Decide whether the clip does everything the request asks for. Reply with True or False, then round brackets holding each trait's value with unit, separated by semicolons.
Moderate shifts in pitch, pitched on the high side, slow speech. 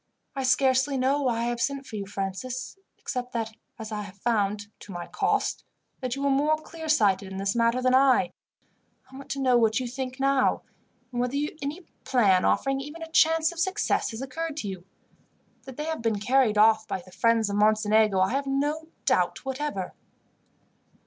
False (4.4 semitones; 255 Hz; 195 wpm)